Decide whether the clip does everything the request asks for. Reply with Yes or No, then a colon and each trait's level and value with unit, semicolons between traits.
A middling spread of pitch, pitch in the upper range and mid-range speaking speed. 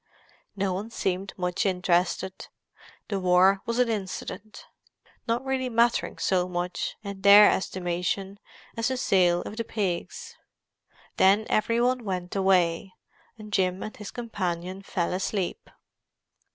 No: average, 3.2 semitones; high, 195 Hz; slow, 130 wpm